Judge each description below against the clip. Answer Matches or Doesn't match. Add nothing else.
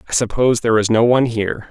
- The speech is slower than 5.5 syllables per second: Doesn't match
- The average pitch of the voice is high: Doesn't match